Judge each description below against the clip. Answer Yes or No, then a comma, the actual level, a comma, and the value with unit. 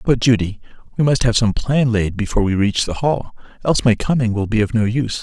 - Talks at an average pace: No, fast, 240 wpm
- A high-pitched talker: No, low, 115 Hz